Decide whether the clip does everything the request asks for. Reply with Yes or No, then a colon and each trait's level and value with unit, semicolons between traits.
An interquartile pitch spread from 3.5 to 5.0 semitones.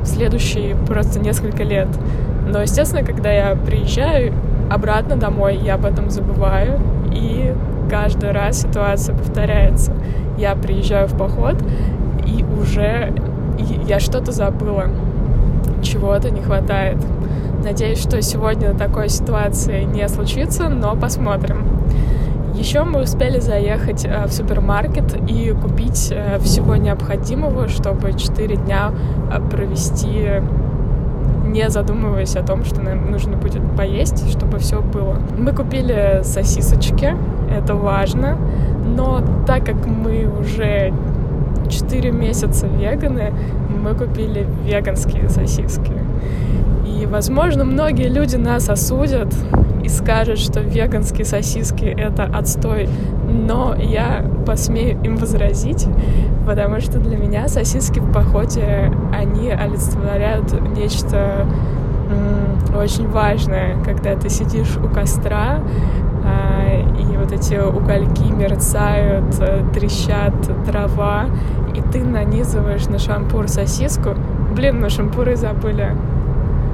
No: average, 2.7 semitones